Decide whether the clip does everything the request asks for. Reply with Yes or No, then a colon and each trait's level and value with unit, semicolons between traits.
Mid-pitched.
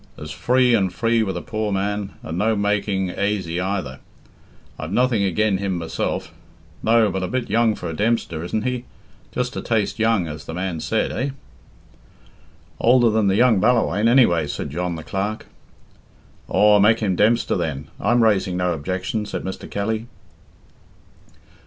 No: low, 100 Hz